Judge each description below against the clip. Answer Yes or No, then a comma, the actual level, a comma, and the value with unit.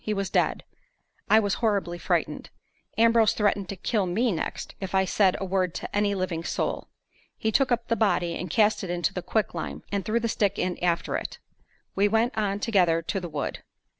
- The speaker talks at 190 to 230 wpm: Yes, average, 200 wpm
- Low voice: No, high, 200 Hz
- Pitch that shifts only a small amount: No, average, 3.3 semitones